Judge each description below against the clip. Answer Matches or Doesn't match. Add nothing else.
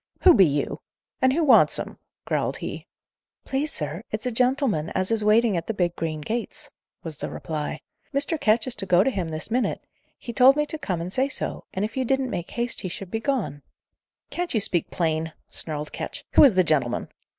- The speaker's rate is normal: Doesn't match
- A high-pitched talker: Matches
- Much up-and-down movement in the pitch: Matches